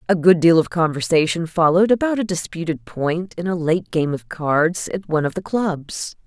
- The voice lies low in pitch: No, medium, 165 Hz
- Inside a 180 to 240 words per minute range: Yes, average, 200 wpm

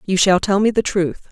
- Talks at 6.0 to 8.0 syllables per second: No, 5.5 syllables/s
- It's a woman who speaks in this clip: Yes, female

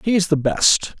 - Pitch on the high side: No, medium, 165 Hz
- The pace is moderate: No, fast, 240 wpm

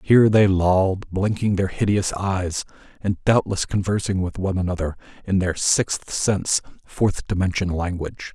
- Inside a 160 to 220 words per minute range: No, average, 145 wpm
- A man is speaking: Yes, male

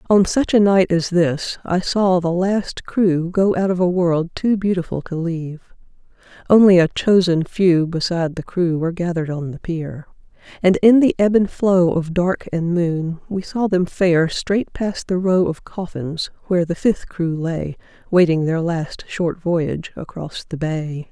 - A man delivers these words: No, female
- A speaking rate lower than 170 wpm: No, average, 185 wpm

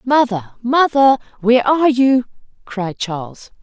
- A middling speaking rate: No, slow, 115 wpm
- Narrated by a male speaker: No, female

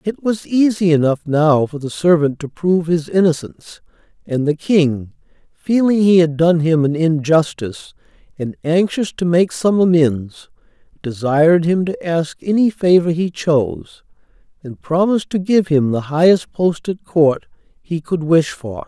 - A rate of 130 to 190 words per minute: Yes, average, 160 wpm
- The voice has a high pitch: No, medium, 165 Hz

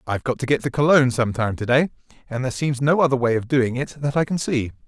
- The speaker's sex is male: Yes, male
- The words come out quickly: Yes, fast, 285 wpm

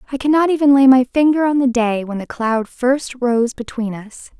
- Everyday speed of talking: No, fast, 220 wpm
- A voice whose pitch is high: Yes, very high, 255 Hz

